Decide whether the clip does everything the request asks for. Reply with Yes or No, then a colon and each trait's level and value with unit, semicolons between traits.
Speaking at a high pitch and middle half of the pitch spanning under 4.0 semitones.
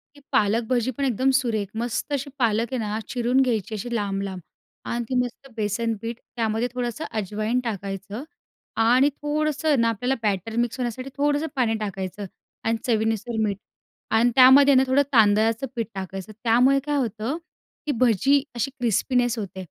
Yes: high, 235 Hz; average, 3.4 semitones